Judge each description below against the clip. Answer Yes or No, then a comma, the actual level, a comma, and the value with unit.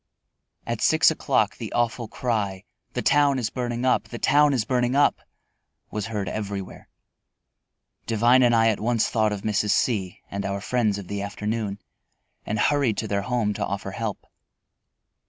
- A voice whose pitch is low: Yes, low, 110 Hz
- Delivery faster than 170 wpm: No, average, 165 wpm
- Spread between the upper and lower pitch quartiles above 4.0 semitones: No, average, 3.2 semitones